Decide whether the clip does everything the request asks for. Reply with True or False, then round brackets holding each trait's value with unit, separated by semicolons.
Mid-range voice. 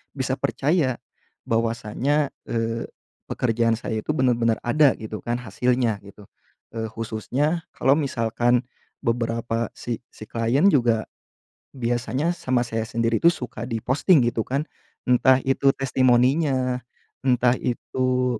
False (125 Hz)